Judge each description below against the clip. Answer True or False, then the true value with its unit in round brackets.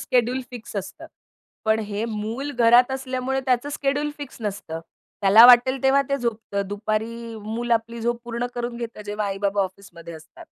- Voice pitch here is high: True (230 Hz)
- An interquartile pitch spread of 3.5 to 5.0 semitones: False (3.1 semitones)